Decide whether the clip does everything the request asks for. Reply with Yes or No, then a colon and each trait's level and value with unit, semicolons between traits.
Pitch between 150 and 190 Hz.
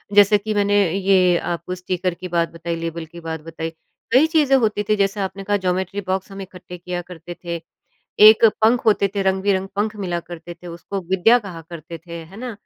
Yes: medium, 185 Hz